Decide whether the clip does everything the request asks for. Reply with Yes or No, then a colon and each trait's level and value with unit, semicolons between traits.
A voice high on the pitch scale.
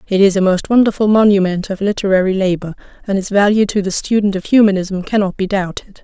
Yes: high, 195 Hz